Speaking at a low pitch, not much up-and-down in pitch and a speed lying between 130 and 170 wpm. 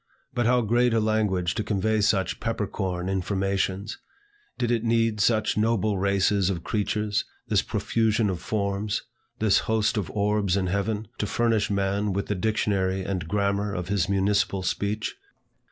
Yes: low, 100 Hz; narrow, 2.1 semitones; average, 155 wpm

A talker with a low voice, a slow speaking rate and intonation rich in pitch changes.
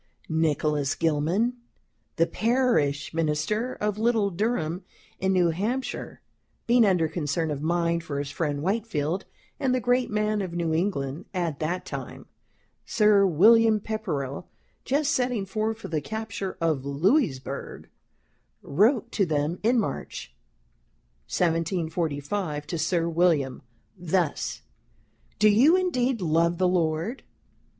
No: medium, 180 Hz; slow, 125 wpm; wide, 5.7 semitones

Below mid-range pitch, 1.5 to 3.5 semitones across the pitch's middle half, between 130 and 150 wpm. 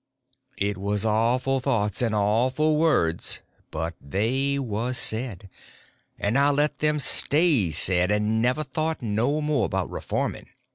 No: low, 120 Hz; wide, 5.4 semitones; slow, 135 wpm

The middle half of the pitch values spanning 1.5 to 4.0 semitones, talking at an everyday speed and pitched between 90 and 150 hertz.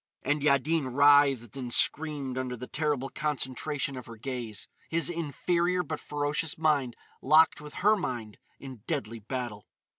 Yes: average, 3.3 semitones; average, 145 wpm; medium, 140 Hz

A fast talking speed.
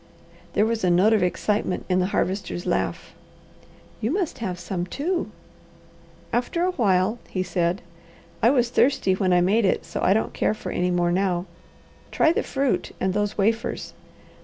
No: average, 170 wpm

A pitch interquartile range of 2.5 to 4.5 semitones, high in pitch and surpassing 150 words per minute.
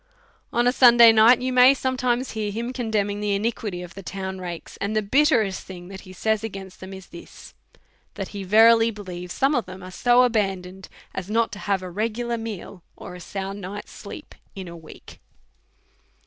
Yes: average, 3.5 semitones; high, 205 Hz; average, 190 wpm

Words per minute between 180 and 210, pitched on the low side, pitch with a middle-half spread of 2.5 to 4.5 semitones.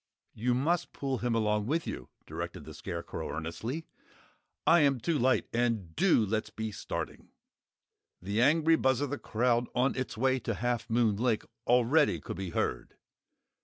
No: average, 165 wpm; low, 120 Hz; average, 3.8 semitones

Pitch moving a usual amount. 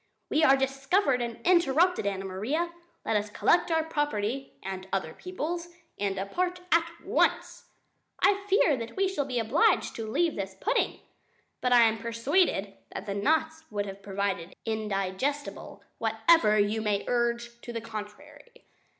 No: wide, 7.6 semitones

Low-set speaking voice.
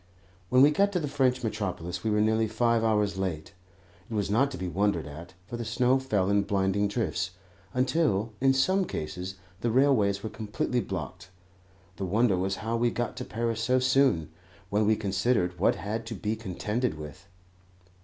Yes: low, 110 Hz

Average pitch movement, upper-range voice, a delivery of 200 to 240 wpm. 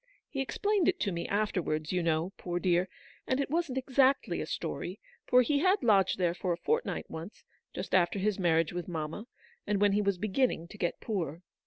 No: wide, 6.8 semitones; high, 195 Hz; fast, 205 wpm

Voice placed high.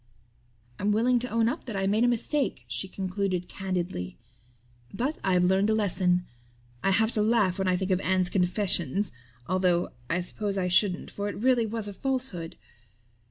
Yes: high, 195 Hz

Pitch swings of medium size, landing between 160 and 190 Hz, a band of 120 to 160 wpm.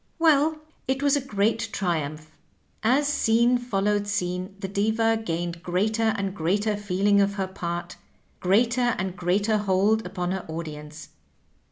No: average, 3.9 semitones; high, 200 Hz; average, 140 wpm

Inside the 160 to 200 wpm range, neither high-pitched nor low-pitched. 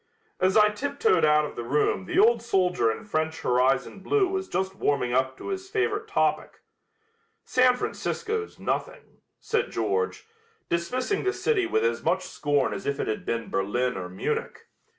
No: average, 170 wpm; high, 195 Hz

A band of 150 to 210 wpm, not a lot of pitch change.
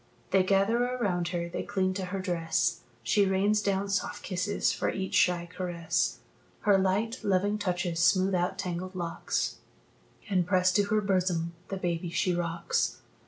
Yes: average, 160 wpm; narrow, 2.2 semitones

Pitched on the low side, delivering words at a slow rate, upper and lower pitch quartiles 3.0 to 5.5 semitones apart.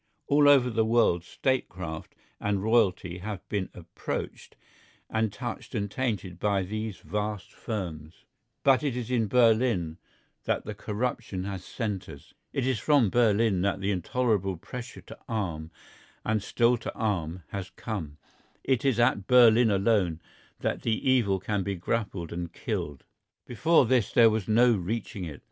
No: low, 105 Hz; average, 150 wpm; average, 4.2 semitones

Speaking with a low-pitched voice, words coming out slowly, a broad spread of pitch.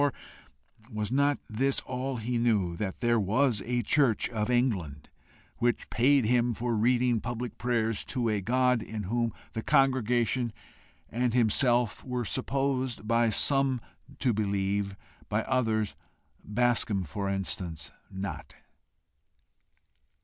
No: low, 120 Hz; slow, 125 wpm; average, 2.9 semitones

